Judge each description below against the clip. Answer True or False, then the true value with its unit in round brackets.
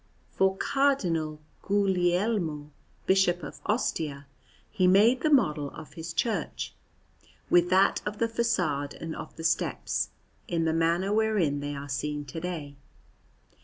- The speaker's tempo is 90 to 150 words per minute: True (135 wpm)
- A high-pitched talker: False (175 Hz)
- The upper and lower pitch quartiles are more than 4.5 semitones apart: True (5.1 semitones)